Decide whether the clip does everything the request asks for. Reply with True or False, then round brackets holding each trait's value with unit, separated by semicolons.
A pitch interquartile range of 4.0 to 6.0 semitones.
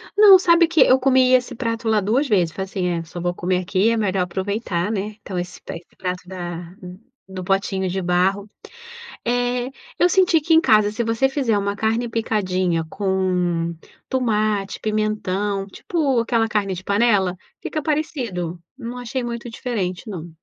True (4.7 semitones)